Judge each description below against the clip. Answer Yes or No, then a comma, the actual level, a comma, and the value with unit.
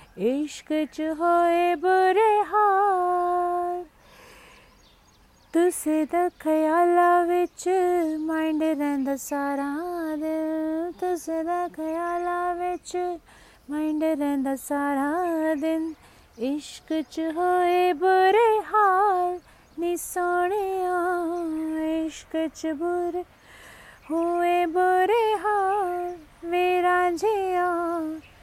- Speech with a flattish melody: Yes, narrow, 2.1 semitones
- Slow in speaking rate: Yes, slow, 60 wpm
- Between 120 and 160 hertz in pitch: No, very high, 345 Hz